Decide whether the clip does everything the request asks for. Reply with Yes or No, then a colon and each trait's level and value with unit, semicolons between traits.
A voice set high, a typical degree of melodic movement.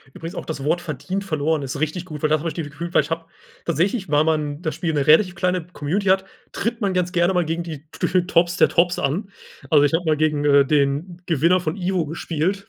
No: medium, 165 Hz; average, 3.1 semitones